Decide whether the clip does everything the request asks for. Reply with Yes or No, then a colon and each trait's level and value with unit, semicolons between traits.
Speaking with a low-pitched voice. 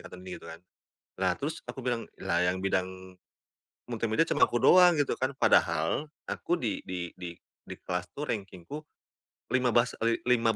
Yes: very low, 95 Hz